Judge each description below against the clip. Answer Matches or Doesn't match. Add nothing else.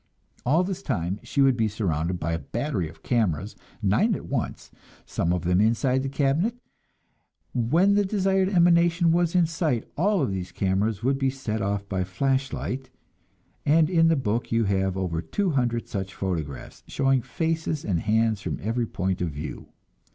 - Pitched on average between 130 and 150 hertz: Doesn't match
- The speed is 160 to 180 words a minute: Matches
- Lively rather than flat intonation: Matches